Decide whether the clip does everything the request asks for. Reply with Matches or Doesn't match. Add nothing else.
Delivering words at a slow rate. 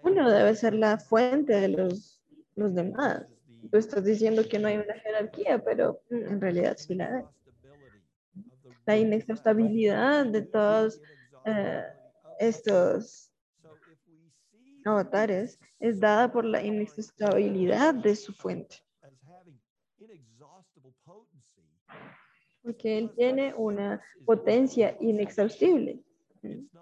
Matches